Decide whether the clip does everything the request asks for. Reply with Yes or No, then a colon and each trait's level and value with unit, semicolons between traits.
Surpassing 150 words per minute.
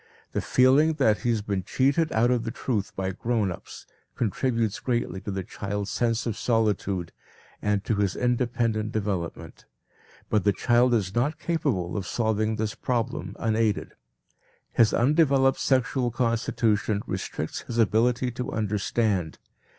No: average, 145 wpm